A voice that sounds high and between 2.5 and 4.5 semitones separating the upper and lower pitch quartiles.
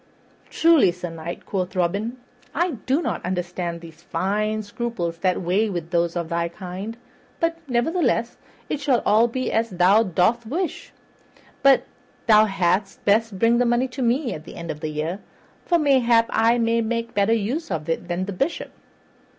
No: high, 210 Hz; average, 5.2 semitones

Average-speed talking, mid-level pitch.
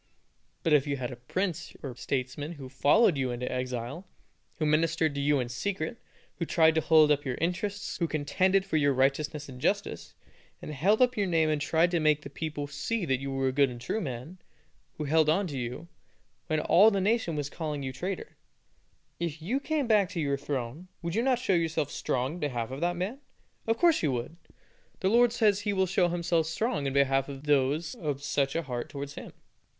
No: fast, 215 wpm; medium, 155 Hz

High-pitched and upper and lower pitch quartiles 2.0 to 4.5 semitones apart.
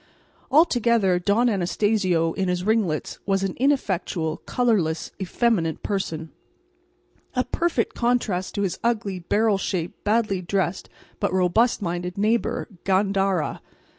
Yes: high, 195 Hz; average, 4.2 semitones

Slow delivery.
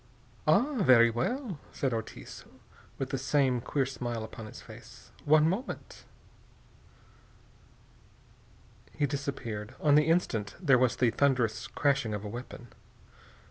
Yes: slow, 125 wpm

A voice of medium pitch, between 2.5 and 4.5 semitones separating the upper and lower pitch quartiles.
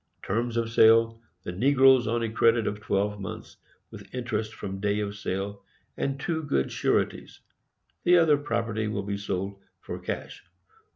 No: low, 110 Hz; average, 2.9 semitones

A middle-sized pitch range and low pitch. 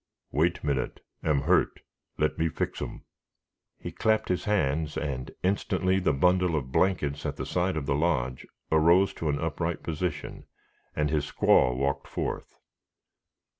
Yes: average, 4.0 semitones; very low, 80 Hz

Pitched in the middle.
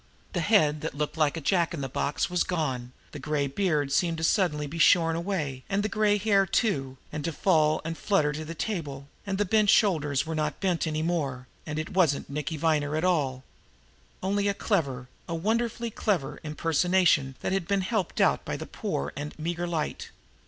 Yes: medium, 165 Hz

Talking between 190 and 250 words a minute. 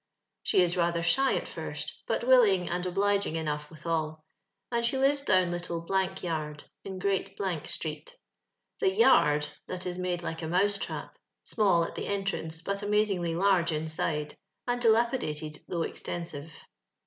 No: average, 150 wpm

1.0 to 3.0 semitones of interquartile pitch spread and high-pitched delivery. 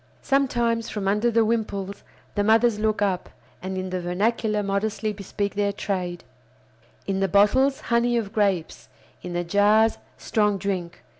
Yes: narrow, 2.4 semitones; high, 205 Hz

